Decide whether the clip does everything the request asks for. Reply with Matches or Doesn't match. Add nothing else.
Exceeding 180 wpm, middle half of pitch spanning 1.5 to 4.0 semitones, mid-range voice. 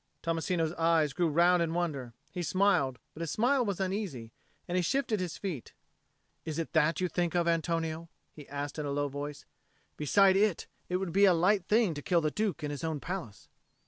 Matches